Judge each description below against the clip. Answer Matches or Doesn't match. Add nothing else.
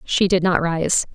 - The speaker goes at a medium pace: Doesn't match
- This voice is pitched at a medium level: Matches